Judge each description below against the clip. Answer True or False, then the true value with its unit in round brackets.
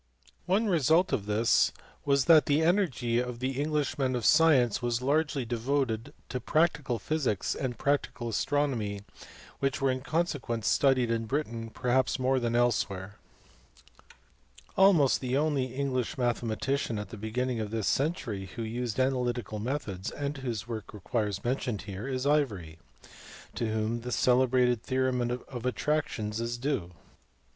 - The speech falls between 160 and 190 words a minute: False (145 wpm)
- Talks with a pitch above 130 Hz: False (125 Hz)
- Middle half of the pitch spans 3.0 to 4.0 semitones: True (3.6 semitones)